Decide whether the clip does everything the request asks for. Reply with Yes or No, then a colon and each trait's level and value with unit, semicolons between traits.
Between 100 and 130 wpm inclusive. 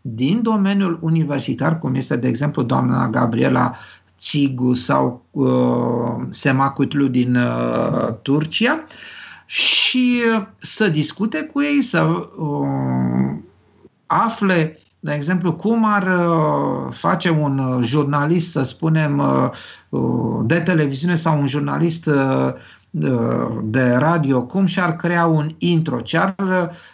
Yes: average, 120 wpm